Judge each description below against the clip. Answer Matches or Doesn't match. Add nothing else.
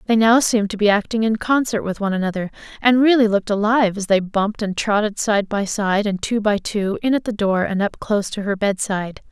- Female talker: Matches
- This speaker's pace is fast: Matches